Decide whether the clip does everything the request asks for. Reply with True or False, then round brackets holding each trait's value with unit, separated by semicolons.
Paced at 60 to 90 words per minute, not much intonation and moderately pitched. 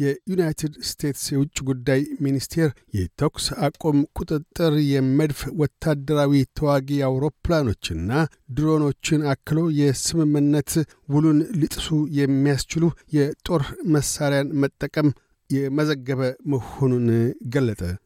True (80 wpm; 2.0 semitones; 145 Hz)